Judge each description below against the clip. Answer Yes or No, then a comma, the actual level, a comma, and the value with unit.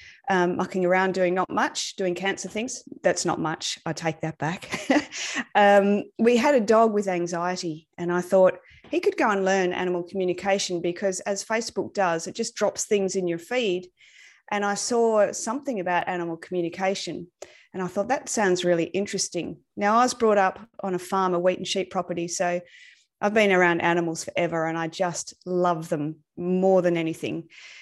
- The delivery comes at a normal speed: Yes, average, 185 wpm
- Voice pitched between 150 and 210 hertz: Yes, medium, 185 Hz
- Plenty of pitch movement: No, average, 2.9 semitones